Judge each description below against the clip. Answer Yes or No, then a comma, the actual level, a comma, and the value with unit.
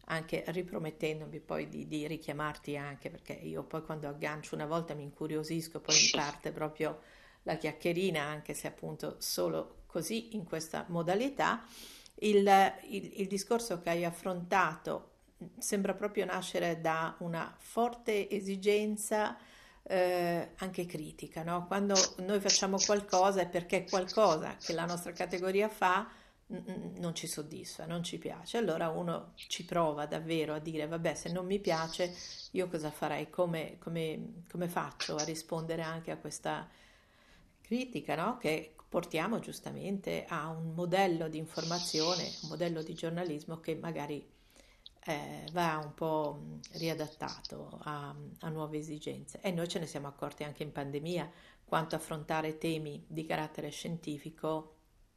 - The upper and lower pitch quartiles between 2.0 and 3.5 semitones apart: Yes, average, 3.1 semitones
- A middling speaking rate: Yes, average, 140 wpm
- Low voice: No, medium, 165 Hz